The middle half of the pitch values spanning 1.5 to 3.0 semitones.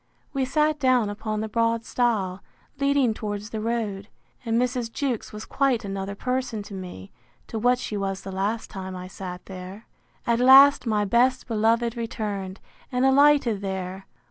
No: average, 4.2 semitones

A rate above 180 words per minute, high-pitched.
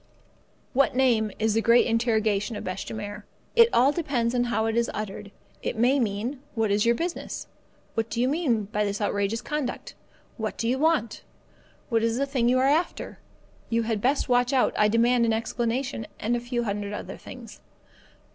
Yes: average, 195 wpm; high, 230 Hz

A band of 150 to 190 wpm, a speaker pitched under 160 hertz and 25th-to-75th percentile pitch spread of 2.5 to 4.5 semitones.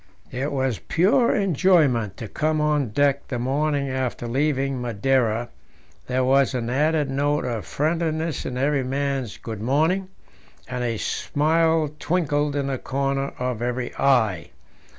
No: average, 140 wpm; low, 135 Hz; average, 3.3 semitones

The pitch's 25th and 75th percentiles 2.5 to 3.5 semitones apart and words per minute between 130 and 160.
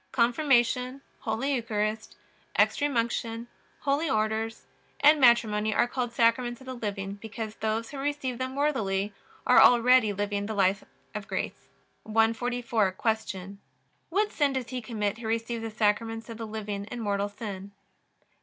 Yes: average, 2.9 semitones; average, 145 wpm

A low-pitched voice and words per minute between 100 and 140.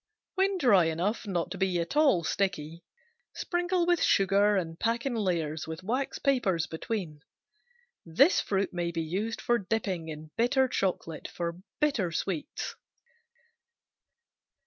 No: high, 190 Hz; slow, 135 wpm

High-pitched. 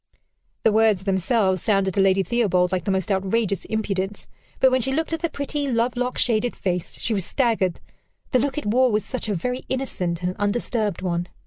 Yes: high, 210 Hz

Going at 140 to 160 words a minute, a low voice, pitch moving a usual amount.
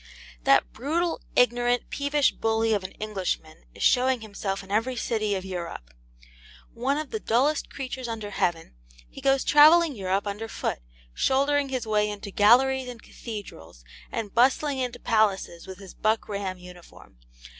No: average, 155 wpm; high, 225 Hz; average, 5.0 semitones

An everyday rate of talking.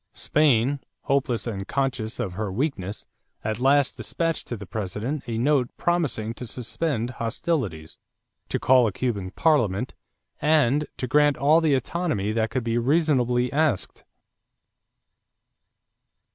No: slow, 130 wpm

